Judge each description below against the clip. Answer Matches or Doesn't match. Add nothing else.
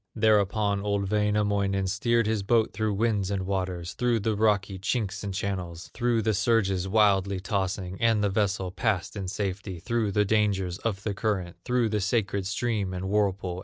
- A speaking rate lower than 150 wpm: Doesn't match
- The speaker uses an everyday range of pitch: Doesn't match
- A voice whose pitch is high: Doesn't match